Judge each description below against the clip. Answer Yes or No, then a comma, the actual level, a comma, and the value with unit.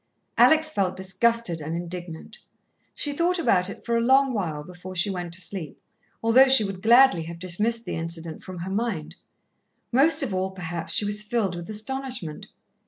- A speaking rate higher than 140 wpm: Yes, average, 175 wpm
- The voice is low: No, high, 190 Hz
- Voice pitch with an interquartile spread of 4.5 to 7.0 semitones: Yes, average, 5.2 semitones